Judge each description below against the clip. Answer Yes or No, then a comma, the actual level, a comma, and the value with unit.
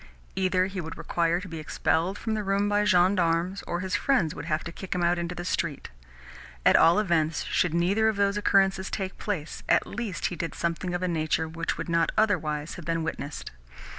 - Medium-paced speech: No, fast, 210 wpm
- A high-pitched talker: No, medium, 175 Hz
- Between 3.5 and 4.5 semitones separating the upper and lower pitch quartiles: No, average, 2.9 semitones